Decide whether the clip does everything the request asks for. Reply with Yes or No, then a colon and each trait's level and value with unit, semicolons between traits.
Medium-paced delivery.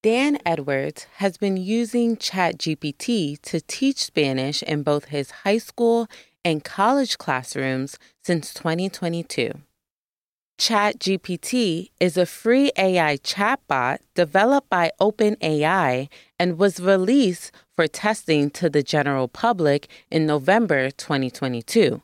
No: slow, 110 wpm